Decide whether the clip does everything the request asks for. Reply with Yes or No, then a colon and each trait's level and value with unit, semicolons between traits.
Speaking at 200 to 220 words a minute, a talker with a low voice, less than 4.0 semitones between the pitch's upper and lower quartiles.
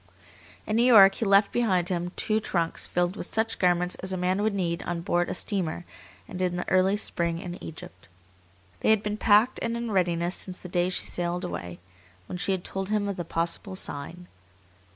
No: fast, 205 wpm; medium, 185 Hz; average, 2.7 semitones